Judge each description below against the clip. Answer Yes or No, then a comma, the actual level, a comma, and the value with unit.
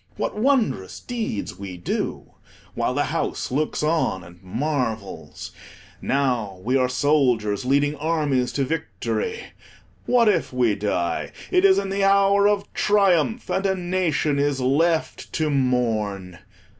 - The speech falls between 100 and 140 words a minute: Yes, slow, 135 wpm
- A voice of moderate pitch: Yes, medium, 145 Hz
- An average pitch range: No, wide, 8.7 semitones